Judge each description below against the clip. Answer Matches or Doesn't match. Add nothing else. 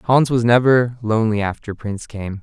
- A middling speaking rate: Matches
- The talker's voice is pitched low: Matches